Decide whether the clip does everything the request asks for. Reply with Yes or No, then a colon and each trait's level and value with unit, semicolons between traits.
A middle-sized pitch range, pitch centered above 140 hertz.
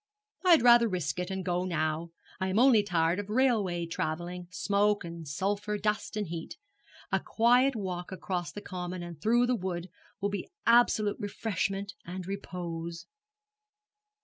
Yes: average, 3.3 semitones; high, 190 Hz